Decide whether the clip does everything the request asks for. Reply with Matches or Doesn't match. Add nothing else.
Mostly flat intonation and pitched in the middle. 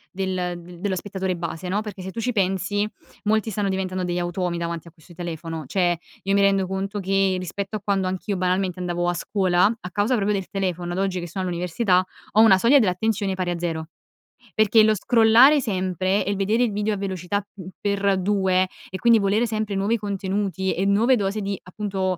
Doesn't match